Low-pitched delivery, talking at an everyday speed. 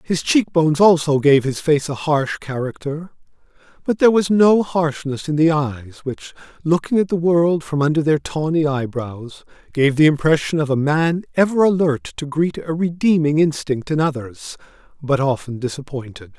No: medium, 150 Hz; average, 165 wpm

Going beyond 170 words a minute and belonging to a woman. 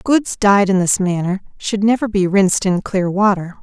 Yes: average, 200 wpm; female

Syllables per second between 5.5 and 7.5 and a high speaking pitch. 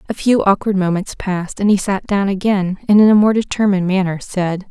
Yes: 5.7 syllables/s; high, 195 Hz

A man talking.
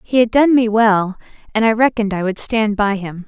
No: female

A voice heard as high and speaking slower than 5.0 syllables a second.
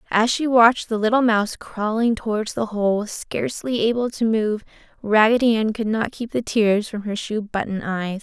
Yes: high, 220 Hz; 4.8 syllables/s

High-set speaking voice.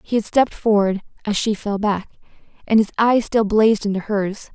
Yes: high, 210 Hz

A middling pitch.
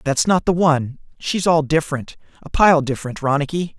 Yes: medium, 155 Hz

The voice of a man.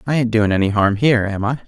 Yes: male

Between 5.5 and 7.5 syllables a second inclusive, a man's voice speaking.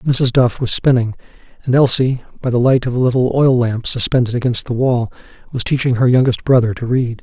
Yes: 5.6 syllables/s; male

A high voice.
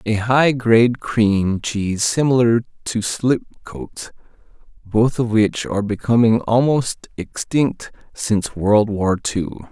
No: low, 110 Hz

